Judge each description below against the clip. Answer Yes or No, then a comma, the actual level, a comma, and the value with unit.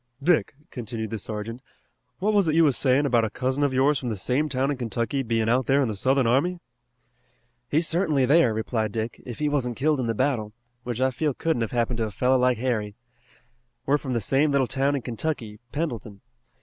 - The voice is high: No, low, 130 Hz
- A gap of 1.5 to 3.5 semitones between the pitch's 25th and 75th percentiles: No, average, 3.9 semitones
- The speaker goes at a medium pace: No, fast, 215 wpm